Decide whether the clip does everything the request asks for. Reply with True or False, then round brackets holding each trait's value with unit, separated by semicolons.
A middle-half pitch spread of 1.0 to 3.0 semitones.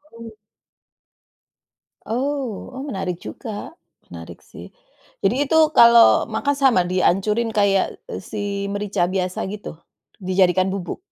False (3.7 semitones)